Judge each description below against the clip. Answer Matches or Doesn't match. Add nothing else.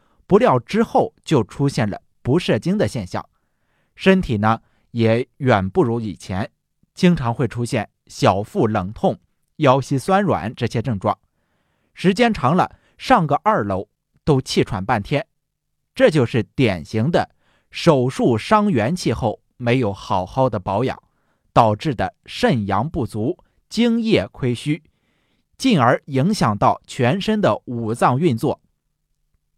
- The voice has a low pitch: Matches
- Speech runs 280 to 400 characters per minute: Doesn't match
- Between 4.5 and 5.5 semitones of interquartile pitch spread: Doesn't match